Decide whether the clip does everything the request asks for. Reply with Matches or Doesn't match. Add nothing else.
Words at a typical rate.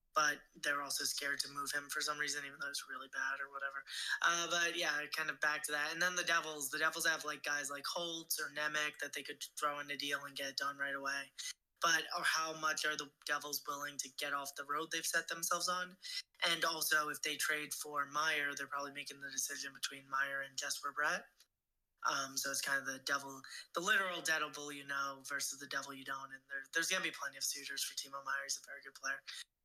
Doesn't match